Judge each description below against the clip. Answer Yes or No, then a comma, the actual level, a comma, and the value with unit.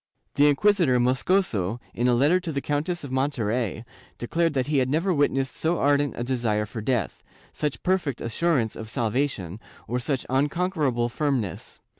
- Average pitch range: Yes, average, 4.1 semitones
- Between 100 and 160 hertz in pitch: Yes, low, 135 Hz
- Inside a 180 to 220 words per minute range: No, average, 160 wpm